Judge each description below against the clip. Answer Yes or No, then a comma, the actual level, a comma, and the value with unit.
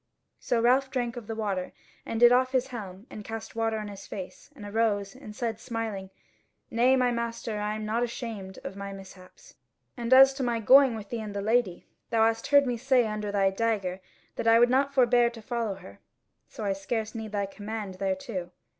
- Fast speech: Yes, fast, 210 wpm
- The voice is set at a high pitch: Yes, high, 225 Hz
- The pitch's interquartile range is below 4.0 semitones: Yes, average, 3.1 semitones